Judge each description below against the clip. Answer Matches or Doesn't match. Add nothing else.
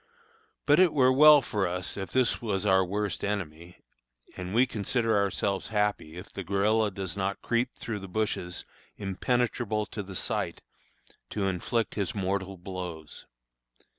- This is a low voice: Matches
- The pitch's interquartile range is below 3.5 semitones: Matches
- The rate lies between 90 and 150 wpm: Matches